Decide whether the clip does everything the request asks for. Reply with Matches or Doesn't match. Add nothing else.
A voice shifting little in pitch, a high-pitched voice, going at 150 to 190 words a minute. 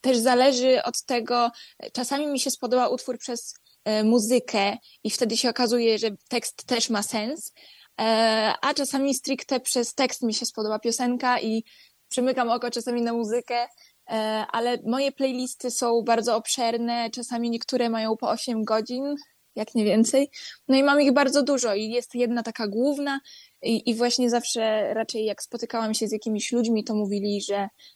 Matches